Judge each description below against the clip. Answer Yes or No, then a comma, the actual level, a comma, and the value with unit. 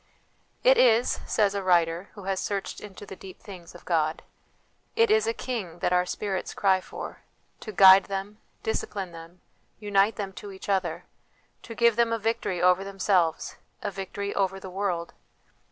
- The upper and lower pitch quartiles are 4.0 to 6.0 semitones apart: No, narrow, 2.4 semitones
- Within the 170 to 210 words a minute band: Yes, average, 180 wpm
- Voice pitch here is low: No, high, 195 Hz